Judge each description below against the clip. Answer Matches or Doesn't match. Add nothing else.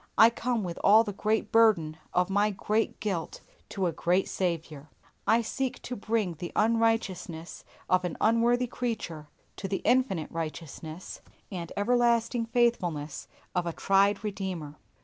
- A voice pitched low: Doesn't match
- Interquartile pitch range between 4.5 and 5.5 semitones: Matches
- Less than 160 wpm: Matches